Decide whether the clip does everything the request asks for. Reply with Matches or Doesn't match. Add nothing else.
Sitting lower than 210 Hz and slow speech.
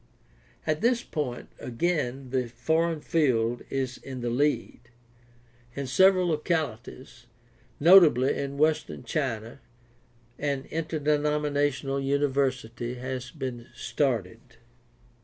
Matches